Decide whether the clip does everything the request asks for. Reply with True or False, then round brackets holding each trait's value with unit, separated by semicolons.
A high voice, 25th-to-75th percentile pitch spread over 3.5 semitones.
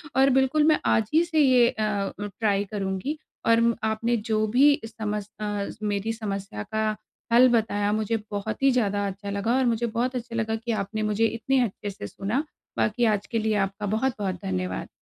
False (220 Hz; 2.7 semitones)